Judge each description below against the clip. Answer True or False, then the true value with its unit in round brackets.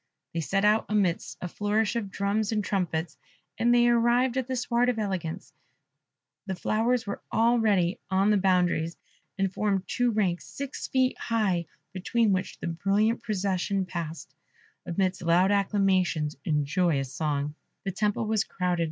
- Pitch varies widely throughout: False (3.9 semitones)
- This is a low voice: False (195 Hz)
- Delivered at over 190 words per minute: False (150 wpm)